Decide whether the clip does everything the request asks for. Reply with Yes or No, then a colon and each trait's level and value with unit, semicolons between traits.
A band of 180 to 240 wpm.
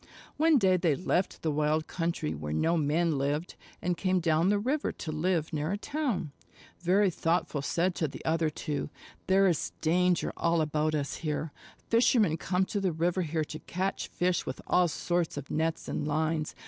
Yes: average, 185 wpm